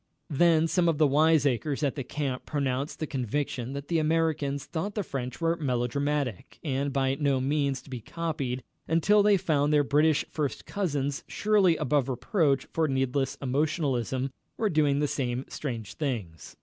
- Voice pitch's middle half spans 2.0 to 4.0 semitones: Yes, average, 3.1 semitones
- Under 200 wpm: Yes, average, 160 wpm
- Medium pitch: Yes, medium, 145 Hz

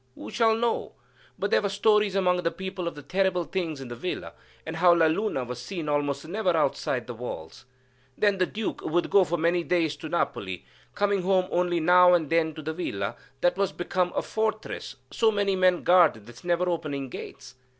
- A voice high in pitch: No, medium, 175 Hz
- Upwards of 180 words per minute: Yes, average, 200 wpm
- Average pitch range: Yes, average, 3.6 semitones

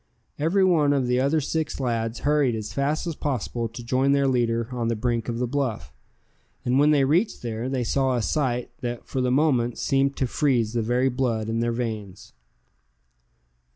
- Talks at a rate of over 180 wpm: Yes, average, 190 wpm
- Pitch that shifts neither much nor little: Yes, average, 3.0 semitones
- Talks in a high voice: No, low, 125 Hz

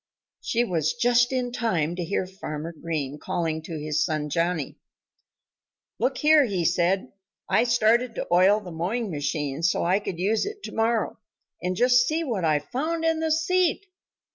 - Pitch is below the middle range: No, high, 195 Hz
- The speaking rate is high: No, average, 170 wpm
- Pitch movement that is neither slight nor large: No, wide, 7.0 semitones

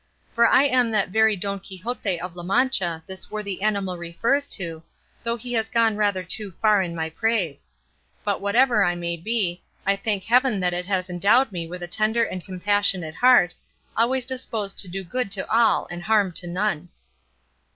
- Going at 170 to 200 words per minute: Yes, average, 185 wpm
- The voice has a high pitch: Yes, high, 200 Hz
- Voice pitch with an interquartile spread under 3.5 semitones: No, average, 4.1 semitones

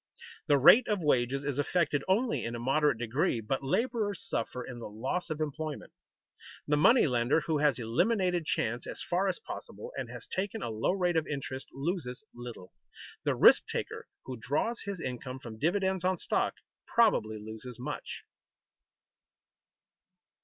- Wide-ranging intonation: Yes, wide, 6.8 semitones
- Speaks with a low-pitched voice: No, medium, 145 Hz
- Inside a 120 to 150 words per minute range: No, average, 160 wpm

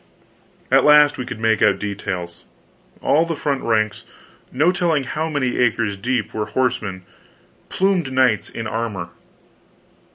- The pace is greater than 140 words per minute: No, slow, 135 wpm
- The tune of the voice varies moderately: No, wide, 5.7 semitones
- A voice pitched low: Yes, low, 120 Hz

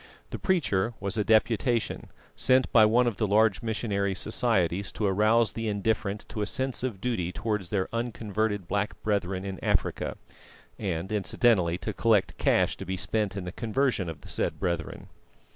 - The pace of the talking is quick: No, average, 170 wpm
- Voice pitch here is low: Yes, low, 105 Hz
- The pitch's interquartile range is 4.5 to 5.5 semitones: No, average, 3.1 semitones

